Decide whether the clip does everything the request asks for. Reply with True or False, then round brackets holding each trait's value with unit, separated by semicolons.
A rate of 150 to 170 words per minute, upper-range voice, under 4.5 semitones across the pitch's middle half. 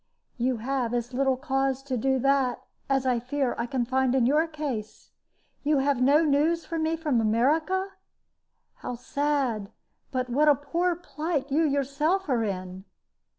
True (160 wpm; 270 Hz; 3.4 semitones)